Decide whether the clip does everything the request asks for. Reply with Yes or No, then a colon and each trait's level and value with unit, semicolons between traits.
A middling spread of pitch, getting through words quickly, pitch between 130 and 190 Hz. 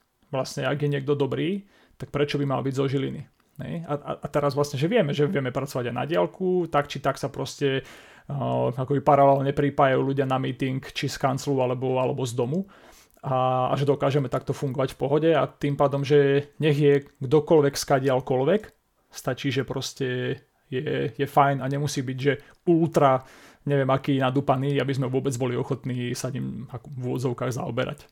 No: narrow, 1.7 semitones; fast, 175 wpm; medium, 140 Hz